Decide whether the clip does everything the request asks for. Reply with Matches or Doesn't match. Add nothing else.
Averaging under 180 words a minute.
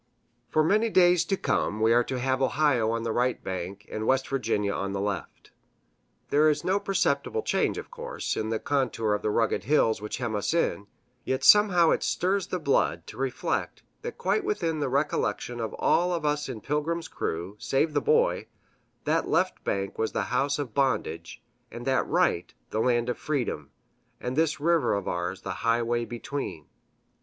Doesn't match